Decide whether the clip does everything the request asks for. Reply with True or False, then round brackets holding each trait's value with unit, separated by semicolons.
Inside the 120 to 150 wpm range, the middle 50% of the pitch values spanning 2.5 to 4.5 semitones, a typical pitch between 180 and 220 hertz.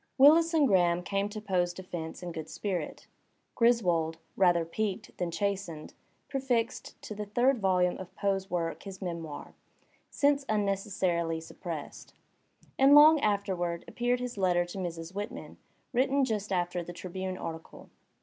True (145 wpm; 3.8 semitones; 190 Hz)